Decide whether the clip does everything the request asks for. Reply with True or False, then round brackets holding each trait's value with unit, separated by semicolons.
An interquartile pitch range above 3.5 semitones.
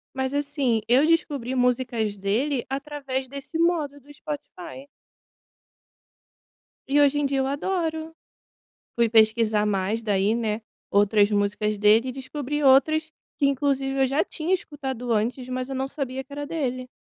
True (4.1 semitones)